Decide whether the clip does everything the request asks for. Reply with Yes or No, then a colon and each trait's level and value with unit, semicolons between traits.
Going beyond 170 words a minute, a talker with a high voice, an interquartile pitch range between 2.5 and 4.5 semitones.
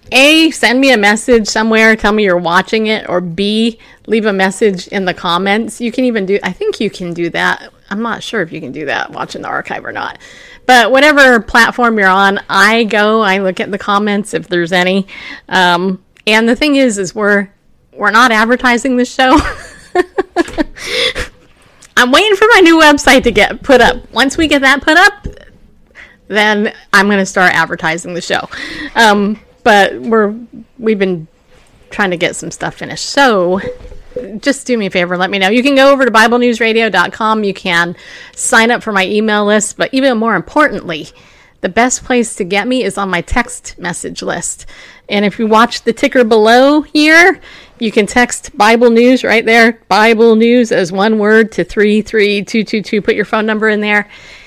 Yes: average, 190 wpm; high, 220 Hz; average, 3.8 semitones